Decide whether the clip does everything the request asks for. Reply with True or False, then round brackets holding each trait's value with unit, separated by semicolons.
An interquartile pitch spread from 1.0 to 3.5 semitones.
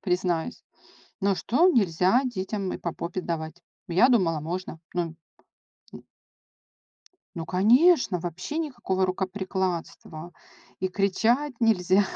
False (4.4 semitones)